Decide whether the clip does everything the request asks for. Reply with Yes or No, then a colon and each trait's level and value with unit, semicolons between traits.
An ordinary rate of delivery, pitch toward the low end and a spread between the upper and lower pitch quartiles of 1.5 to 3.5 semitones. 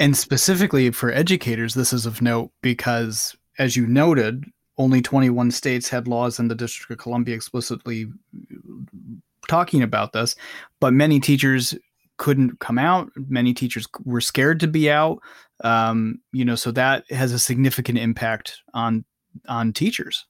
Yes: average, 150 wpm; low, 125 Hz; narrow, 2.6 semitones